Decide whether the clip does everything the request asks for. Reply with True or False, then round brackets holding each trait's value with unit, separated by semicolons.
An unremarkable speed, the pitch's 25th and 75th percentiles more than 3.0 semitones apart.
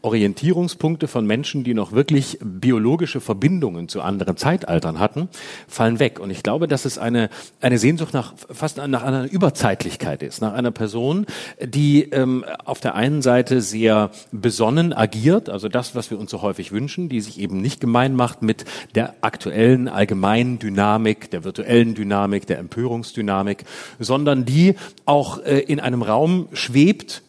True (160 wpm; 4.7 semitones)